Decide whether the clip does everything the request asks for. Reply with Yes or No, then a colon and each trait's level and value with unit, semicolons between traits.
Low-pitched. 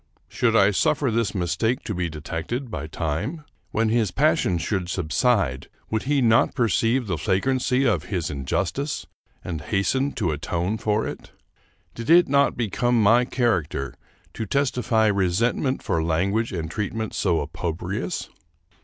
Yes: low, 105 Hz